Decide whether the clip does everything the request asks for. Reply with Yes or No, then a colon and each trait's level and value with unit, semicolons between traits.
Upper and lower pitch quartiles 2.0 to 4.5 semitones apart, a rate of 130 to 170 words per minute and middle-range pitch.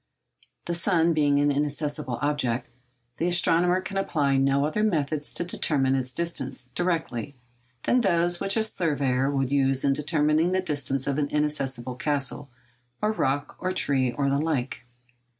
Yes: average, 3.9 semitones; average, 150 wpm; medium, 145 Hz